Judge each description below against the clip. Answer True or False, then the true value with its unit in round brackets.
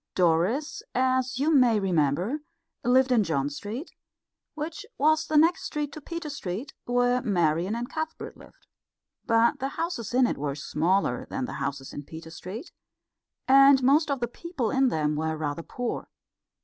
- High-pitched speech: True (245 Hz)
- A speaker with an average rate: True (160 wpm)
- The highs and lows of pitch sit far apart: True (8.4 semitones)